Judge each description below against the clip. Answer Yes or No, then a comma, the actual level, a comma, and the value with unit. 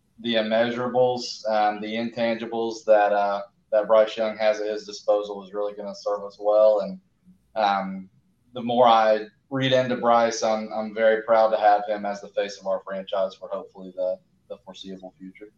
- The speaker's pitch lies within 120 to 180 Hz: No, low, 105 Hz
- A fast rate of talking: No, average, 185 wpm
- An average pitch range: No, narrow, 2.0 semitones